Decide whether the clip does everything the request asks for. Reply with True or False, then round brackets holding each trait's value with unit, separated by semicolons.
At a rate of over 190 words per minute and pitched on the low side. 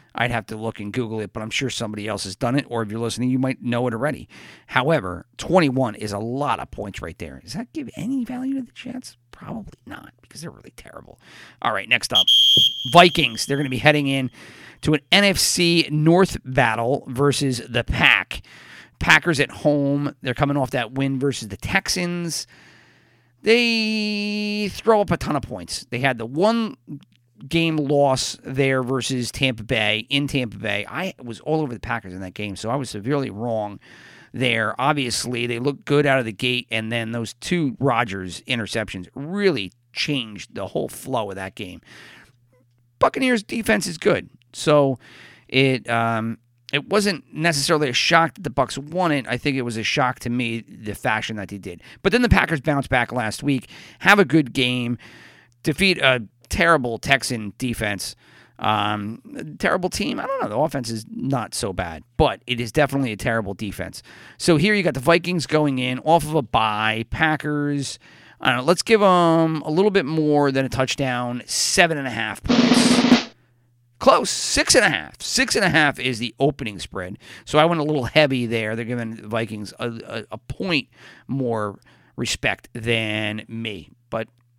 False (185 wpm; 130 Hz)